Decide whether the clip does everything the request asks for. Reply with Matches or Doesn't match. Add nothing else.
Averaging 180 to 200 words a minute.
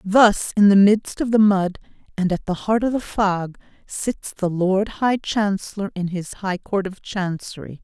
Matches